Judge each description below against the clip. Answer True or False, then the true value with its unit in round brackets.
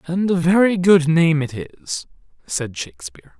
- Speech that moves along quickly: False (160 wpm)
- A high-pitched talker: False (150 Hz)